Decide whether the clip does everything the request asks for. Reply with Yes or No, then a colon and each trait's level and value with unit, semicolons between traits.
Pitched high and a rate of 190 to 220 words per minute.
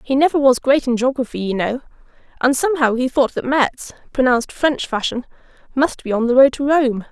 Yes: very high, 260 Hz; fast, 205 wpm